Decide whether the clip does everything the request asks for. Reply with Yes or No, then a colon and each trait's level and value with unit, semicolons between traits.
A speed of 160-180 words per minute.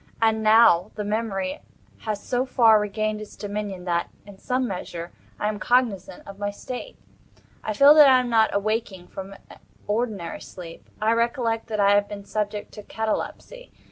Yes: average, 170 wpm